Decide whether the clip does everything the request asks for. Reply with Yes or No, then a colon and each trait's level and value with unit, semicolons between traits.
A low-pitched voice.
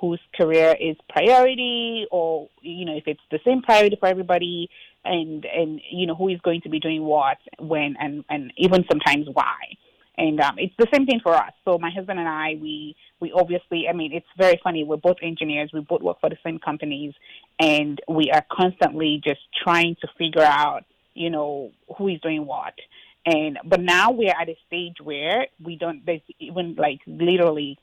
No: medium, 165 Hz